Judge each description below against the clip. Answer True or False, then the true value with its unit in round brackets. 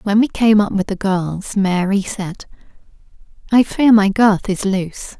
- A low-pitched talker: False (200 Hz)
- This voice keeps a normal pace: True (175 wpm)